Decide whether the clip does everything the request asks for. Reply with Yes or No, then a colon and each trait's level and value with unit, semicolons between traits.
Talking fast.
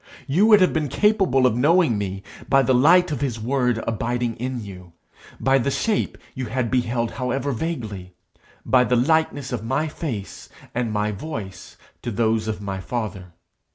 No: average, 170 wpm